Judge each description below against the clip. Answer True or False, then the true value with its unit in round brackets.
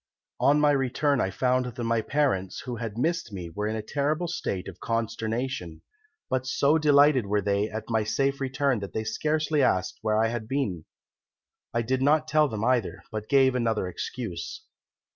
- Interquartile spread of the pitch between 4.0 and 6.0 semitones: True (4.6 semitones)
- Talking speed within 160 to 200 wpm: True (180 wpm)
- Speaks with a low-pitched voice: True (120 Hz)